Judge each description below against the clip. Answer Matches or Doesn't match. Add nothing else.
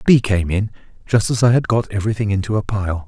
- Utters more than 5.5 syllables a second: Matches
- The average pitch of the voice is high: Doesn't match